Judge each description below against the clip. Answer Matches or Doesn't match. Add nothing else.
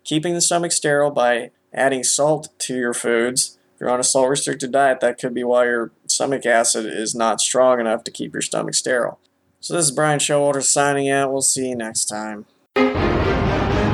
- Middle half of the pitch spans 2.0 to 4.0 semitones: Matches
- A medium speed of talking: Matches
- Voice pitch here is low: Matches